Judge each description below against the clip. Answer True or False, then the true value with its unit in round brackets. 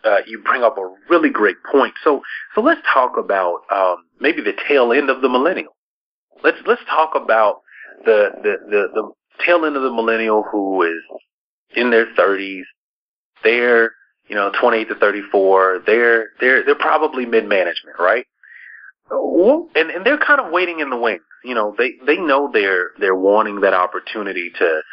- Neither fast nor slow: True (180 wpm)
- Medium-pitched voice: False (120 Hz)